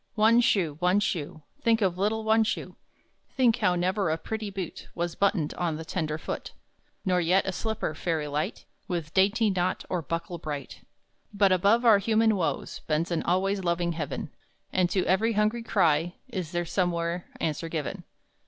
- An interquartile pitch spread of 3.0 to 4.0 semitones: Yes, average, 3.7 semitones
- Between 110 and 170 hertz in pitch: No, medium, 180 Hz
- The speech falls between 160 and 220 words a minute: Yes, average, 170 wpm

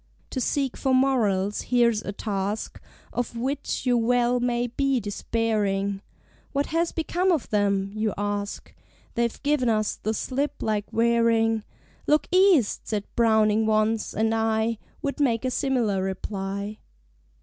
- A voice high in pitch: Yes, high, 225 Hz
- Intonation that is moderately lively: Yes, average, 3.4 semitones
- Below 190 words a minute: Yes, average, 140 wpm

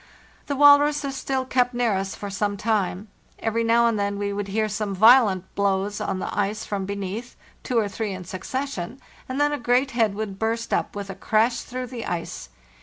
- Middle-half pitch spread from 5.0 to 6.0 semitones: No, average, 3.7 semitones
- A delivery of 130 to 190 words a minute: No, average, 200 wpm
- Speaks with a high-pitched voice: Yes, high, 220 Hz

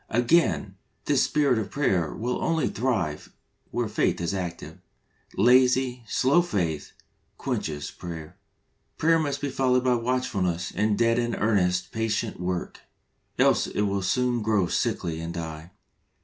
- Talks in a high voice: No, low, 110 Hz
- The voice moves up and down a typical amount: No, wide, 6.0 semitones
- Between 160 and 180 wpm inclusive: No, slow, 135 wpm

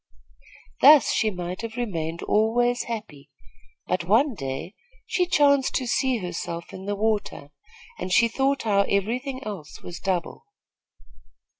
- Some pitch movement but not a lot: No, wide, 5.7 semitones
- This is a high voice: Yes, high, 215 Hz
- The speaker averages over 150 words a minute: No, average, 140 wpm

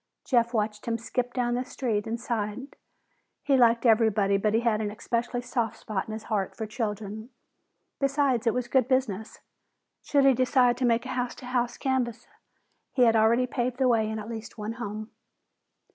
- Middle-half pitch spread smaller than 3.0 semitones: Yes, narrow, 2.4 semitones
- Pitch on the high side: Yes, high, 235 Hz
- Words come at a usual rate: Yes, average, 190 wpm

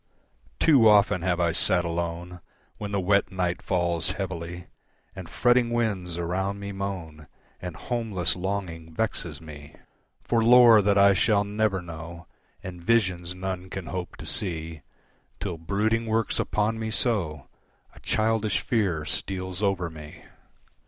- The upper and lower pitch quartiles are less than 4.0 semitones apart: Yes, average, 3.6 semitones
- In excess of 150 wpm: No, average, 140 wpm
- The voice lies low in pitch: Yes, very low, 95 Hz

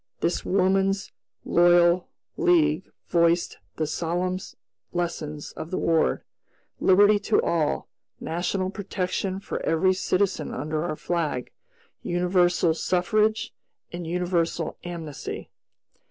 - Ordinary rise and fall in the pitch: No, narrow, 2.1 semitones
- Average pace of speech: No, slow, 100 wpm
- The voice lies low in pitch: No, medium, 175 Hz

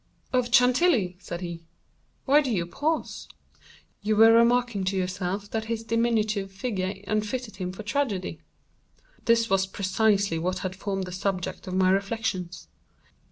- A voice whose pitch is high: Yes, high, 200 Hz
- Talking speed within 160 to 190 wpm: No, average, 150 wpm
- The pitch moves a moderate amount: Yes, average, 3.6 semitones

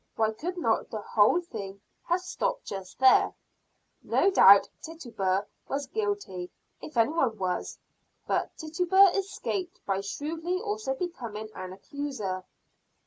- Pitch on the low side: No, very high, 275 Hz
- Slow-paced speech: Yes, slow, 130 wpm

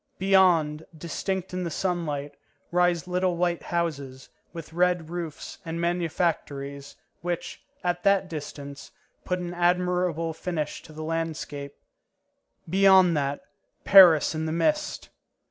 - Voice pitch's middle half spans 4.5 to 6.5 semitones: No, narrow, 2.6 semitones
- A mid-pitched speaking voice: Yes, medium, 170 Hz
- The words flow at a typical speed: No, slow, 120 wpm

